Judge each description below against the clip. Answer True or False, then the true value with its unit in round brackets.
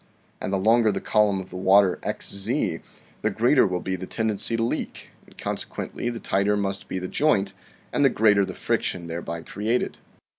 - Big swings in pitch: False (3.0 semitones)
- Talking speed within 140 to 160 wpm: False (185 wpm)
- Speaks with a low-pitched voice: True (100 Hz)